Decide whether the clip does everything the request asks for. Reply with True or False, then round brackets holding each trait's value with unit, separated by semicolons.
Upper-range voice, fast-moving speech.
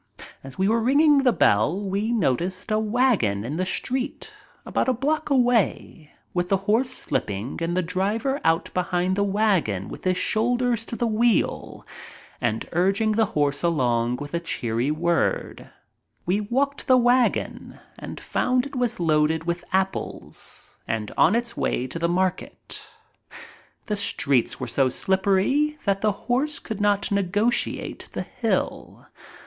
False (195 Hz; 150 wpm)